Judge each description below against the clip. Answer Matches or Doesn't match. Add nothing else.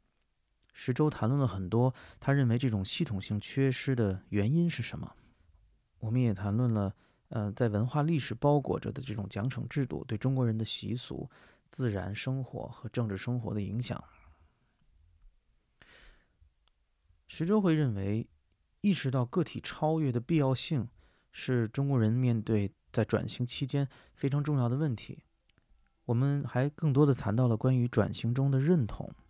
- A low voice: Matches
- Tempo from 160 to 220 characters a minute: Doesn't match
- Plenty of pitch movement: Doesn't match